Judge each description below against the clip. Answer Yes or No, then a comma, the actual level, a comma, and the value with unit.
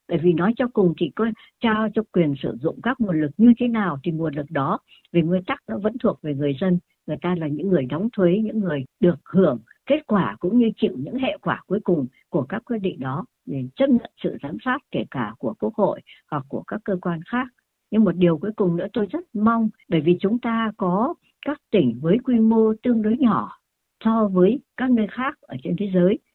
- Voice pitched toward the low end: No, high, 205 Hz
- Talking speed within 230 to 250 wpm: Yes, average, 240 wpm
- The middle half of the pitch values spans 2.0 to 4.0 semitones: No, average, 4.8 semitones